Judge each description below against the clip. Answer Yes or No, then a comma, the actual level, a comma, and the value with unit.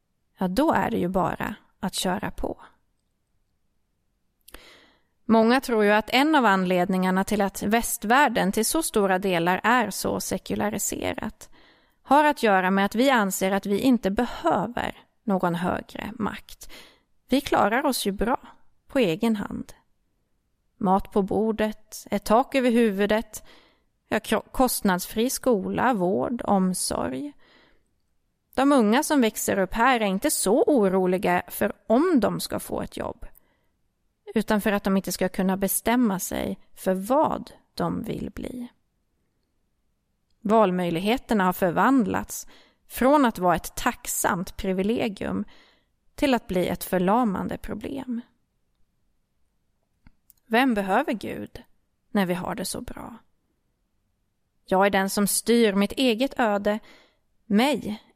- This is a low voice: No, high, 210 Hz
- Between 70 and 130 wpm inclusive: Yes, slow, 125 wpm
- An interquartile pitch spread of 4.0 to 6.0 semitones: Yes, average, 4.4 semitones